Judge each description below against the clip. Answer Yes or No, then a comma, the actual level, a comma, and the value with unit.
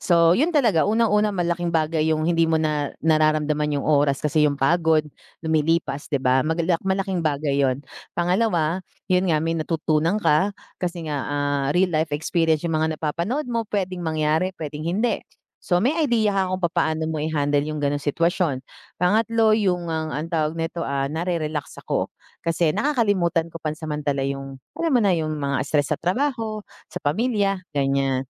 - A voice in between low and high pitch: Yes, medium, 160 Hz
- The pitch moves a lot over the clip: No, average, 3.5 semitones